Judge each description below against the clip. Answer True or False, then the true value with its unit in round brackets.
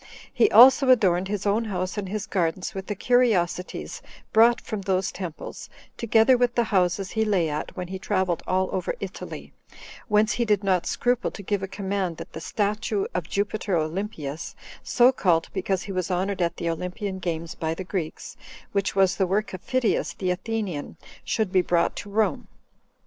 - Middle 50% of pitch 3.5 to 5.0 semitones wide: False (3.0 semitones)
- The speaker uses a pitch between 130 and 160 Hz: False (195 Hz)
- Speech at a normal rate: True (180 wpm)